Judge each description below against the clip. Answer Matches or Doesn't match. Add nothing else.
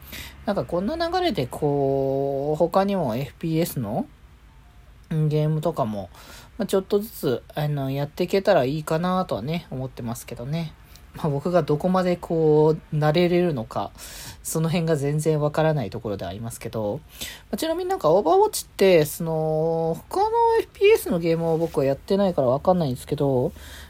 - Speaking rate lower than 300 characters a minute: Doesn't match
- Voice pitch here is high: Doesn't match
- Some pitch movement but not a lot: Matches